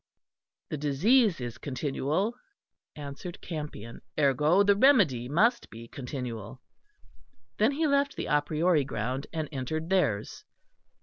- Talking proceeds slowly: Yes, slow, 120 wpm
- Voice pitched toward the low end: No, medium, 150 Hz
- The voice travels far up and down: Yes, wide, 6.8 semitones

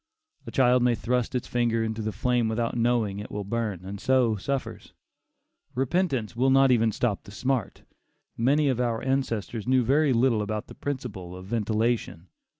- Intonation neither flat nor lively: Yes, average, 3.1 semitones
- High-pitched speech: No, low, 120 Hz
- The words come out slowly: No, average, 170 wpm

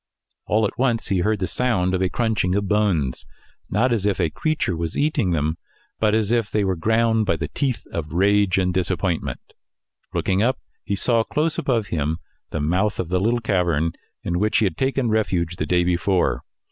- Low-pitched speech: Yes, low, 100 Hz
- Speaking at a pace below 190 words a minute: No, average, 195 wpm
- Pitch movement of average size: Yes, average, 4.2 semitones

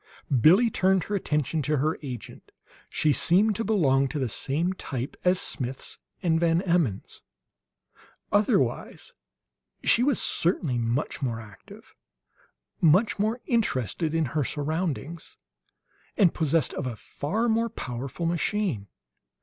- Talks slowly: Yes, slow, 130 wpm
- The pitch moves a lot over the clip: Yes, wide, 6.1 semitones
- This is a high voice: No, medium, 160 Hz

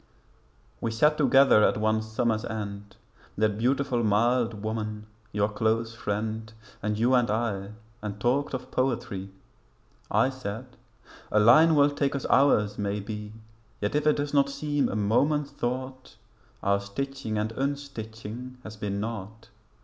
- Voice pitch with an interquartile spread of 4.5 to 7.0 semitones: No, average, 4.0 semitones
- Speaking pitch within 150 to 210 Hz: No, low, 115 Hz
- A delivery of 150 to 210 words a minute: No, average, 140 wpm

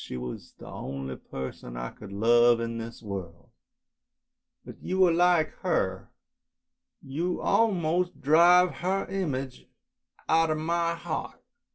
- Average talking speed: No, slow, 130 wpm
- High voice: No, medium, 155 Hz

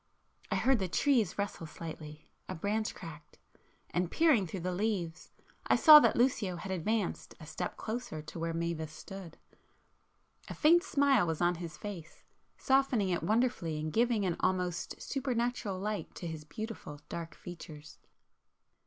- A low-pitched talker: No, medium, 185 Hz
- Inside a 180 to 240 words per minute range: No, average, 145 wpm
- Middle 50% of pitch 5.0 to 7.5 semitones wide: Yes, wide, 5.4 semitones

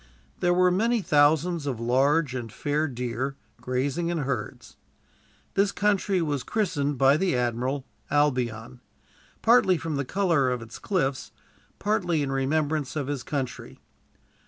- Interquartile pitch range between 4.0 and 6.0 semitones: Yes, average, 5.1 semitones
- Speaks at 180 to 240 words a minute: No, slow, 135 wpm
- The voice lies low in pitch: No, medium, 145 Hz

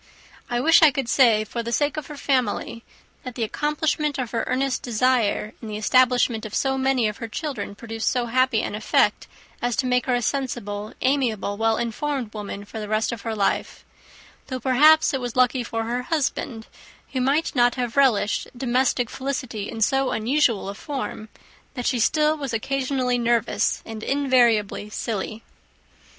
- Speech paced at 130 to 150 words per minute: No, average, 175 wpm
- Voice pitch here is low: No, high, 245 Hz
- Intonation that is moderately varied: Yes, average, 3.3 semitones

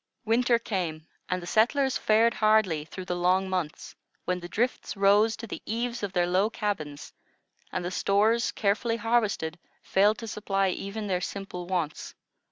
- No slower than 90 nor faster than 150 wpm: No, average, 165 wpm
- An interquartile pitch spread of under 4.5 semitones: Yes, average, 3.7 semitones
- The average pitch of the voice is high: Yes, high, 200 Hz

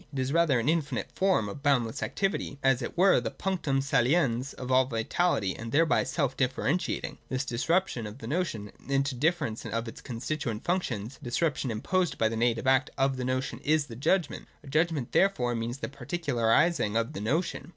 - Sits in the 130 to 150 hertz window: Yes, low, 135 Hz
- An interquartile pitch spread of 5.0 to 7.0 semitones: Yes, average, 5.3 semitones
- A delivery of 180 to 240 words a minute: Yes, average, 195 wpm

